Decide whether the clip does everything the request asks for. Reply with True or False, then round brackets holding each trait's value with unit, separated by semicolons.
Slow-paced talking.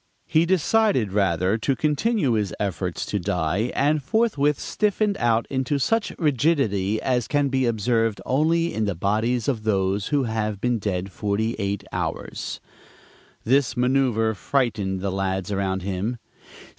False (145 wpm)